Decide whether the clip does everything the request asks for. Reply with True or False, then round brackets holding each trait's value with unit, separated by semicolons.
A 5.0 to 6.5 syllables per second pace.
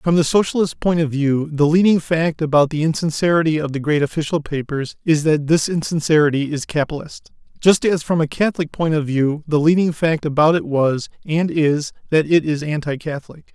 True (5.4 syllables/s)